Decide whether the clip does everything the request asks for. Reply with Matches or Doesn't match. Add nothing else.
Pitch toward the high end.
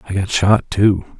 Doesn't match